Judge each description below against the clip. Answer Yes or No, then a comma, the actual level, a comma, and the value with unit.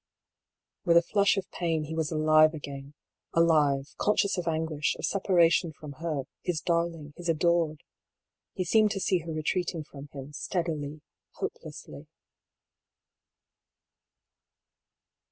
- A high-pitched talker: No, medium, 160 Hz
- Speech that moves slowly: Yes, slow, 125 wpm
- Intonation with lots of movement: No, narrow, 2.4 semitones